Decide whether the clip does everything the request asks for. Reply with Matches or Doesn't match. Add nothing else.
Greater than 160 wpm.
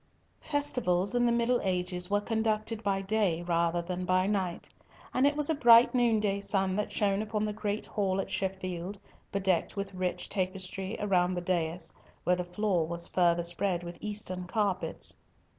Matches